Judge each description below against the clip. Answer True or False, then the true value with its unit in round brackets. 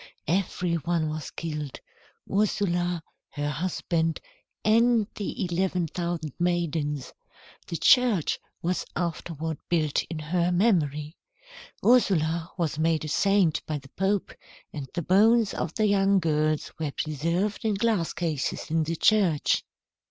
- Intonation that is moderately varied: True (3.9 semitones)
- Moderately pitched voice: True (170 Hz)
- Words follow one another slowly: True (130 wpm)